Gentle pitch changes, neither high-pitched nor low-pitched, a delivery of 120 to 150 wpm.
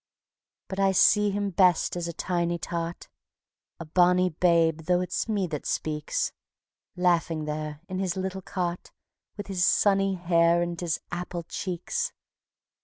Yes: narrow, 2.1 semitones; medium, 175 Hz; average, 145 wpm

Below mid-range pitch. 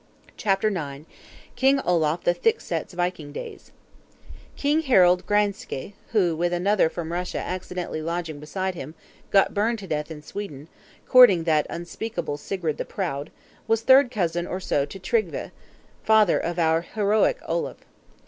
No: medium, 180 Hz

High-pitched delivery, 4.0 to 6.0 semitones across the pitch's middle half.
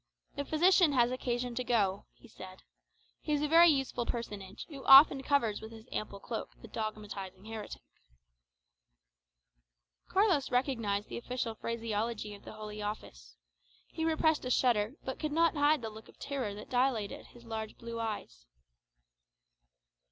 Yes: high, 235 Hz; average, 4.6 semitones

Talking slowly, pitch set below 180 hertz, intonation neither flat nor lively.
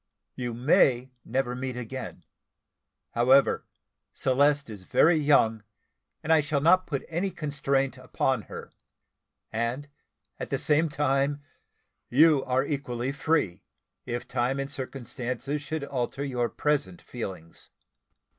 Yes: slow, 120 wpm; low, 135 Hz; average, 3.0 semitones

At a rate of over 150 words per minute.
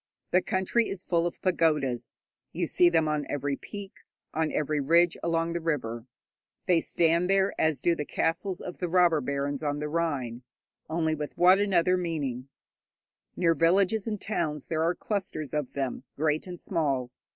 Yes: average, 170 wpm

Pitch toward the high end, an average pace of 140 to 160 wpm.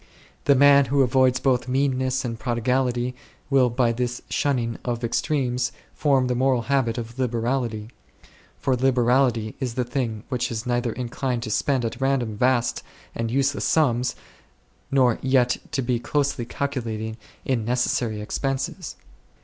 No: low, 125 Hz; average, 150 wpm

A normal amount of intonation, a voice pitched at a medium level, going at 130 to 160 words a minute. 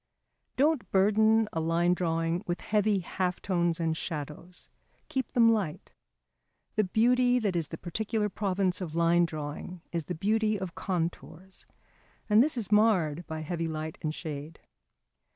Yes: average, 4.5 semitones; medium, 180 Hz; average, 150 wpm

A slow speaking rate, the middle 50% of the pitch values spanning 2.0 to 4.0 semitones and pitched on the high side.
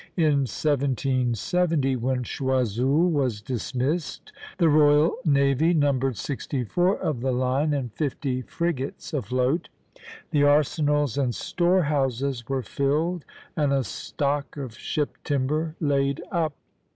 No: slow, 115 wpm; average, 2.8 semitones; medium, 140 Hz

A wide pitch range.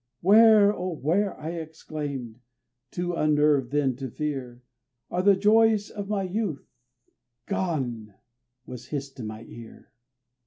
Yes: wide, 6.7 semitones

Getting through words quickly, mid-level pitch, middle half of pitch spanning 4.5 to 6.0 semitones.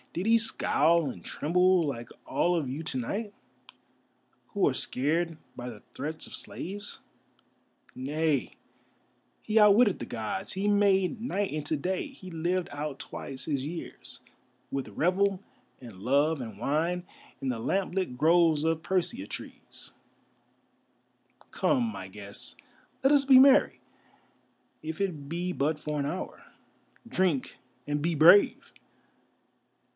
No: slow, 135 wpm; medium, 165 Hz; average, 5.0 semitones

